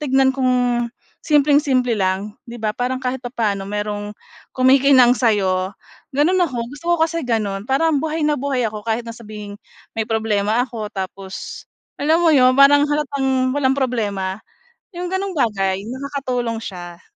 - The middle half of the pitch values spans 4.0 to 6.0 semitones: Yes, average, 4.8 semitones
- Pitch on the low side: No, high, 245 Hz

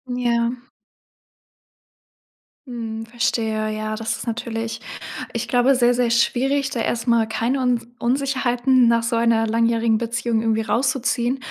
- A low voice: No, high, 235 Hz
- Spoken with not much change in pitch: Yes, narrow, 1.6 semitones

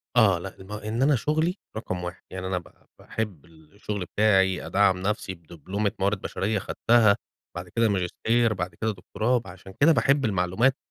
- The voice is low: Yes, low, 100 Hz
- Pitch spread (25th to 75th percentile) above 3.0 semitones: Yes, average, 3.5 semitones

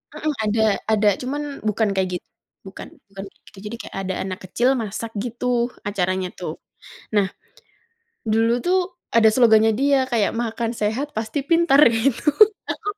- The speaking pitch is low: No, high, 225 Hz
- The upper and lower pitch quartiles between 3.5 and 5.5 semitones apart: Yes, average, 3.8 semitones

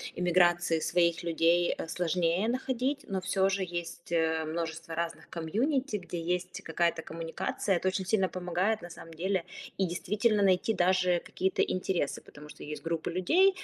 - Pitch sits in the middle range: Yes, medium, 175 Hz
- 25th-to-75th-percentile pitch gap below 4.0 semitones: Yes, narrow, 2.4 semitones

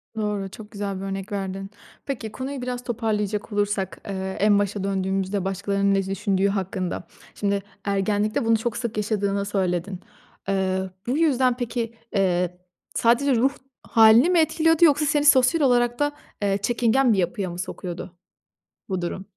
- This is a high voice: Yes, high, 205 Hz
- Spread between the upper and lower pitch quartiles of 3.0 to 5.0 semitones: Yes, average, 3.9 semitones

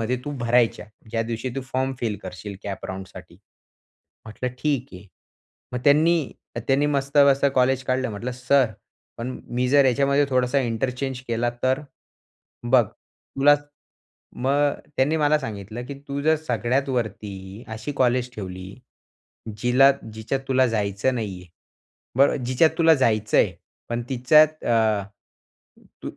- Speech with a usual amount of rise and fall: Yes, average, 3.7 semitones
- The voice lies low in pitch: Yes, low, 125 Hz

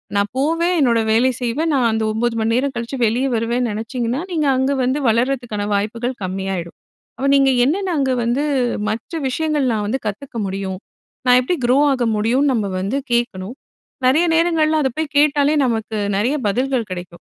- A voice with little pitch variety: No, average, 4.0 semitones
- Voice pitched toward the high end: Yes, high, 245 Hz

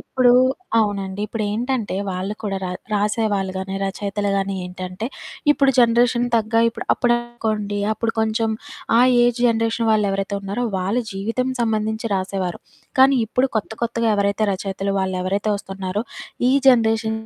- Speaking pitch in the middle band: No, high, 215 Hz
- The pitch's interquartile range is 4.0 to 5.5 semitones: No, average, 2.8 semitones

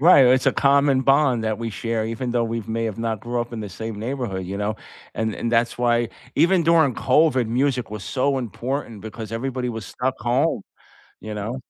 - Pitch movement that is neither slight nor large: Yes, average, 3.0 semitones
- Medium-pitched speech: No, low, 120 Hz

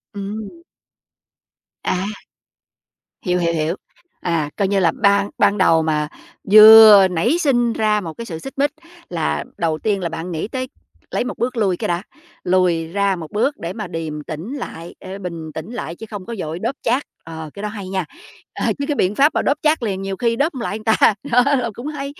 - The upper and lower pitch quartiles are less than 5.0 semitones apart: No, wide, 5.6 semitones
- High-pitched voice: Yes, high, 200 Hz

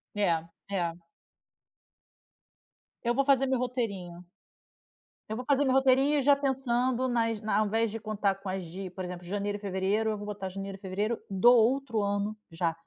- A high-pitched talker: Yes, high, 215 Hz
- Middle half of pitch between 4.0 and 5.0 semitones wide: Yes, average, 4.4 semitones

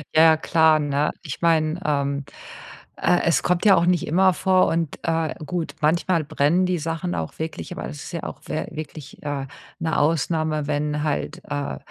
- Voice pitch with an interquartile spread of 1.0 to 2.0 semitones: No, narrow, 2.4 semitones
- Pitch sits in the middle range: Yes, medium, 155 Hz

